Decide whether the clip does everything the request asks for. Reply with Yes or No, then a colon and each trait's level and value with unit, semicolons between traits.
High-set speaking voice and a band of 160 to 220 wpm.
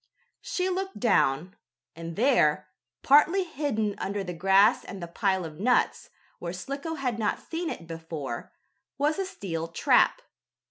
No: high, 205 Hz; average, 145 wpm